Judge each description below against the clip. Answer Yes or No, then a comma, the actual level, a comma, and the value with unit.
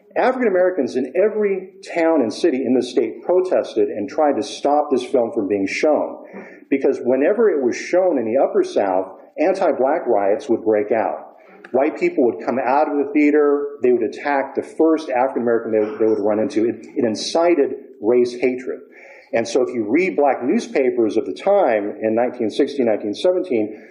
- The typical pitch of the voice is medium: Yes, medium, 170 Hz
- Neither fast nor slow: Yes, average, 180 wpm